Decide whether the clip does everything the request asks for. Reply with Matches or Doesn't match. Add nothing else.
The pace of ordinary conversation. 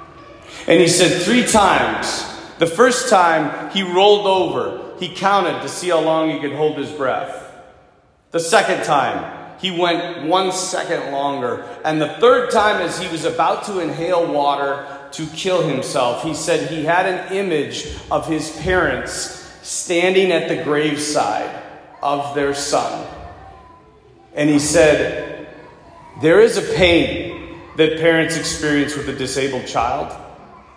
Matches